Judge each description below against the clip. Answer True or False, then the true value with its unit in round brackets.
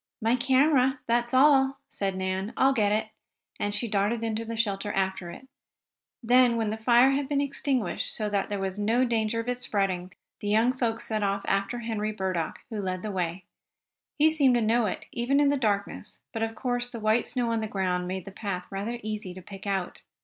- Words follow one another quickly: True (210 wpm)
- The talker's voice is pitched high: True (220 Hz)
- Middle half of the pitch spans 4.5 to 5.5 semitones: False (3.7 semitones)